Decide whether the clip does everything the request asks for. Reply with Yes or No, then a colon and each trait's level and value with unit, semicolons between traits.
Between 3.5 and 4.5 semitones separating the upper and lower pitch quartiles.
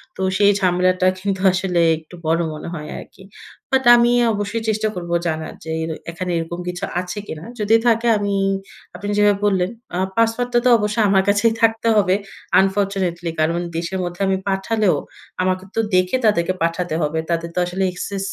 No: average, 3.1 semitones